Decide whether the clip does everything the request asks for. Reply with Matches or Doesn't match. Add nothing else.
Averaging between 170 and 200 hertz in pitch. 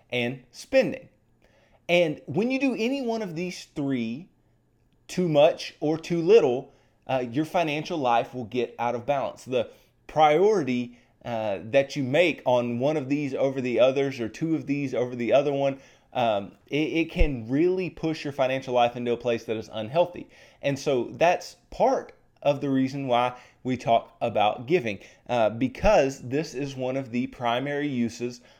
Doesn't match